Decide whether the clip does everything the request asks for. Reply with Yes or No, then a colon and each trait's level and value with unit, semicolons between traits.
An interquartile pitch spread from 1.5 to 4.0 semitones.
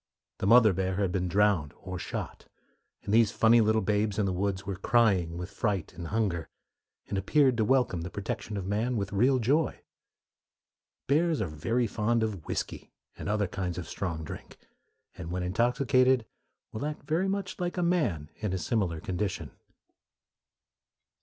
No: average, 4.5 semitones